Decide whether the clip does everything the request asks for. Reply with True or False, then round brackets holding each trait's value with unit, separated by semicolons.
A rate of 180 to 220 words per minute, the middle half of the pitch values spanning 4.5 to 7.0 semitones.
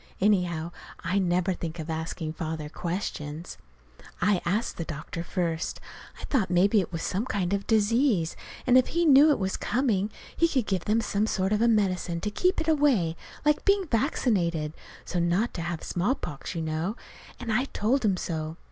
True (185 wpm; 5.4 semitones)